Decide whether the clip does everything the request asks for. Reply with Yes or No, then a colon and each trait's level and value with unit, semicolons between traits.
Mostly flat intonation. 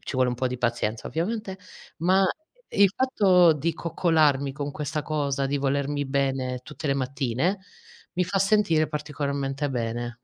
No: average, 3.9 semitones